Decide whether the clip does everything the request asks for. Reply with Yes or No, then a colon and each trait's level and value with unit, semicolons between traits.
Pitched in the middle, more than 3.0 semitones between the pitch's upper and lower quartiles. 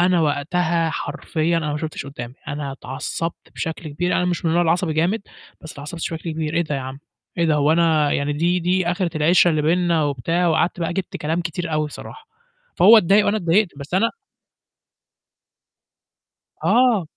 No: medium, 165 Hz; average, 2.7 semitones